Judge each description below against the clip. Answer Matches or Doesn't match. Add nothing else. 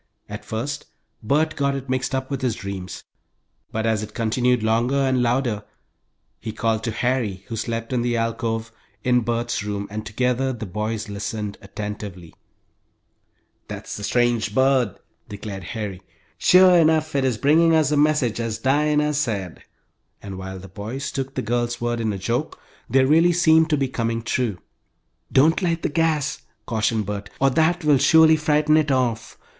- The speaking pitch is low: Matches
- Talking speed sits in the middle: Matches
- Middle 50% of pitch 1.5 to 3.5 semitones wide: Doesn't match